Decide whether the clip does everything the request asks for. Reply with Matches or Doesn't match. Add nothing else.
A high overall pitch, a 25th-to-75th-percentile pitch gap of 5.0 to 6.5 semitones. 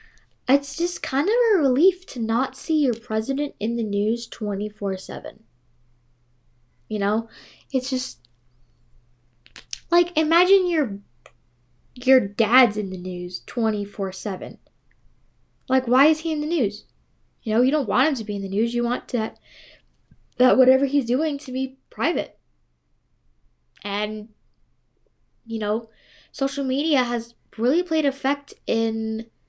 Matches